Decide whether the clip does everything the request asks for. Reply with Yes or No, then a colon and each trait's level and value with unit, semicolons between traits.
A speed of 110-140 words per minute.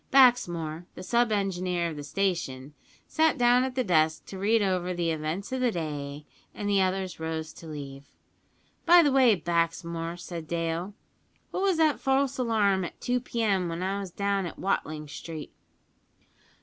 No: average, 170 wpm